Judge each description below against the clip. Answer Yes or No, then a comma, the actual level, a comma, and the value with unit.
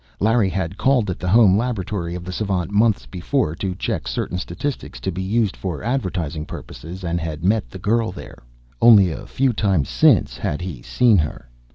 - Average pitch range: Yes, average, 4.2 semitones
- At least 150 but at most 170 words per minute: No, average, 190 wpm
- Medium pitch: No, very low, 95 Hz